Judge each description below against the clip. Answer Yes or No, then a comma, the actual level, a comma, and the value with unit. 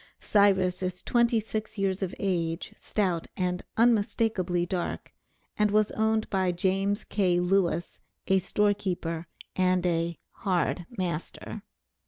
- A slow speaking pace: Yes, slow, 125 wpm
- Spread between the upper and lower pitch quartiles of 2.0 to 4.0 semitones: Yes, narrow, 2.6 semitones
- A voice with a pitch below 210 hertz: Yes, high, 190 Hz